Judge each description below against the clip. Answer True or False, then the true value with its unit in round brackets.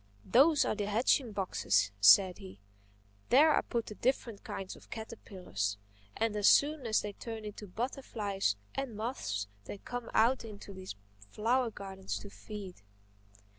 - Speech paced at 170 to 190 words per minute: False (150 wpm)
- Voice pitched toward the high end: True (210 Hz)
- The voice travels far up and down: False (3.7 semitones)